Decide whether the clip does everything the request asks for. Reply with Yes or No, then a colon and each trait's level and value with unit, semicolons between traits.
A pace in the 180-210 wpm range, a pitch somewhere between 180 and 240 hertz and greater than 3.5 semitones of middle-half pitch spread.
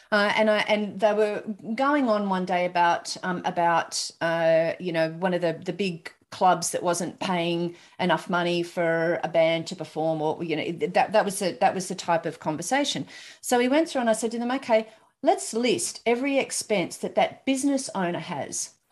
Yes: fast, 205 wpm; medium, 185 Hz; average, 4.7 semitones